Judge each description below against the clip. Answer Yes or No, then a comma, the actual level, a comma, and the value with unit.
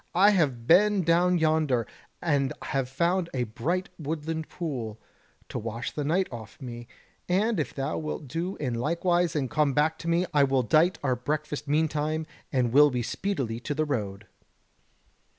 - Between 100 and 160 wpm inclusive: No, average, 170 wpm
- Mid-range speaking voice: Yes, medium, 150 Hz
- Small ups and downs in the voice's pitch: No, average, 5.1 semitones